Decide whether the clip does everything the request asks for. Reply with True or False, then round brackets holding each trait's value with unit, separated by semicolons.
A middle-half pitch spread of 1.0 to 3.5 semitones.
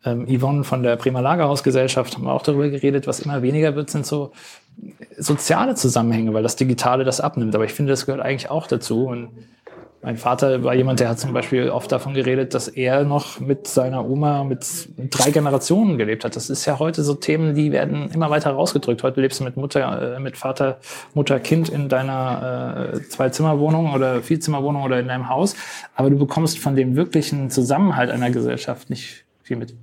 True (2.5 semitones)